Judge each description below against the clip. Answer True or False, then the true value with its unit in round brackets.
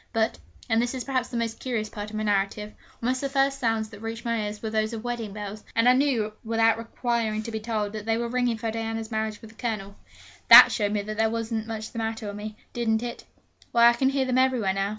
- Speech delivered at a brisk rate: True (245 wpm)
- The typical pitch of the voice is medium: False (225 Hz)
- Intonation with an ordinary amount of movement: False (1.8 semitones)